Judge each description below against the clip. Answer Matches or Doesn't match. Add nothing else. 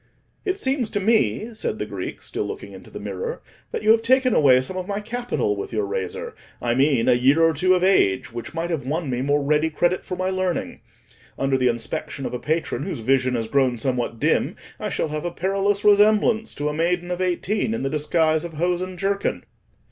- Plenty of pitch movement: Matches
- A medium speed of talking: Doesn't match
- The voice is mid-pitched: Matches